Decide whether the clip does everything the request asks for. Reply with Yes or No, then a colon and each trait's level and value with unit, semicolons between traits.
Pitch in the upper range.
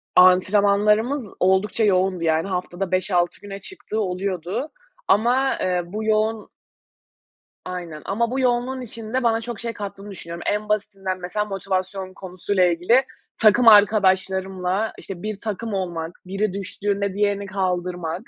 Yes: high, 195 Hz